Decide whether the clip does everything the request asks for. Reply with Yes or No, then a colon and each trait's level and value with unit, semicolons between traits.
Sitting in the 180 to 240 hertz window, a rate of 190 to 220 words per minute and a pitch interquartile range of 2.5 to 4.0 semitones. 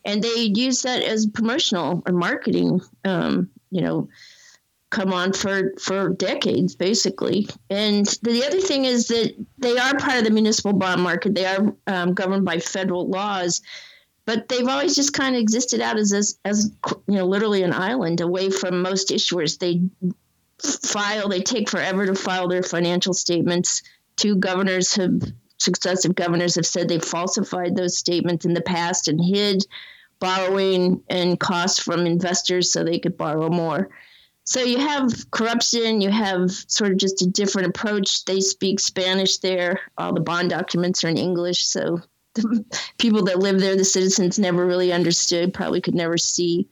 No: high, 190 Hz; average, 170 wpm; average, 2.9 semitones